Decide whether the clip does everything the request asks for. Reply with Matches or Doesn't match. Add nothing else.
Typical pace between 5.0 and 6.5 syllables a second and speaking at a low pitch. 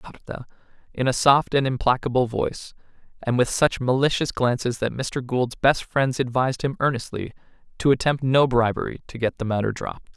Matches